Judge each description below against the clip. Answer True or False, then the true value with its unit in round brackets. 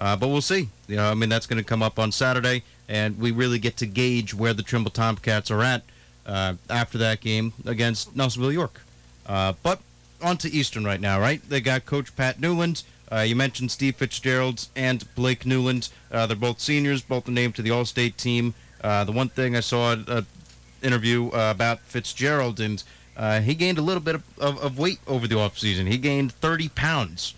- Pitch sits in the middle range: False (120 Hz)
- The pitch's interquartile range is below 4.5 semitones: True (3.2 semitones)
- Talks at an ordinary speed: False (210 wpm)